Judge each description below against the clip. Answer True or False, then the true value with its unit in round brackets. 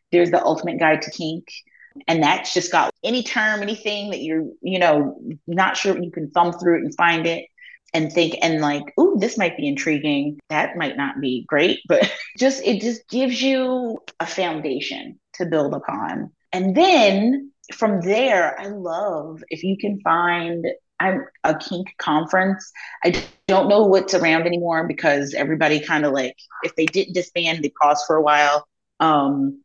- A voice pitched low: False (175 Hz)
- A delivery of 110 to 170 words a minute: False (180 wpm)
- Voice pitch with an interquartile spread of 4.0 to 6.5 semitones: True (4.8 semitones)